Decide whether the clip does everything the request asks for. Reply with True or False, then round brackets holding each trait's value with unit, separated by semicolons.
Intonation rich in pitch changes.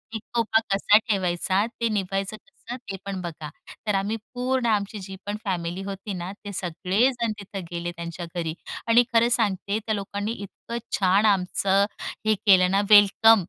False (2.7 semitones)